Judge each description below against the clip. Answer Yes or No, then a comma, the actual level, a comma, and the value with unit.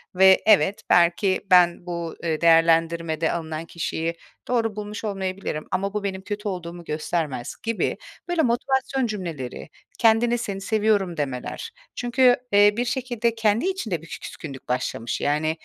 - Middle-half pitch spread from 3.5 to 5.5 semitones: Yes, average, 5.0 semitones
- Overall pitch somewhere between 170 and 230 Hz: Yes, high, 190 Hz